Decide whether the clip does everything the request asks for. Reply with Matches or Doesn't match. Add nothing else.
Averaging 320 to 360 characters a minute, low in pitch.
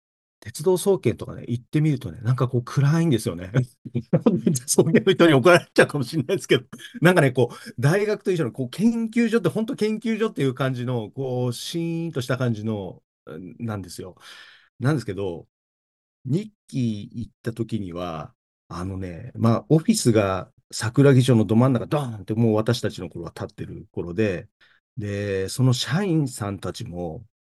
Matches